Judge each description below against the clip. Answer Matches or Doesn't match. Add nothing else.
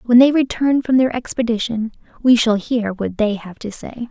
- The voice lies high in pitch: Matches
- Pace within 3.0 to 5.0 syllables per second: Matches